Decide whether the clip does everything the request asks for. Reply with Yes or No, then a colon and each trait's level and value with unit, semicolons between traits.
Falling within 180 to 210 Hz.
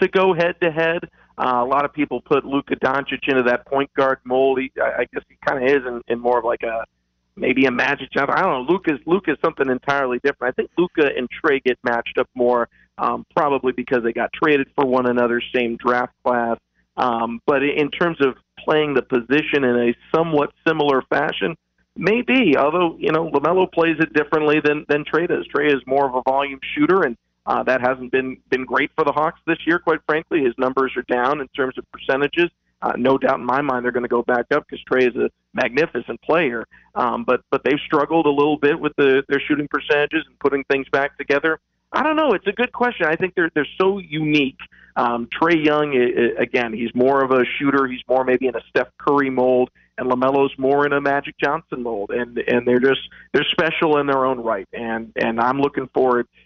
No: medium, 140 Hz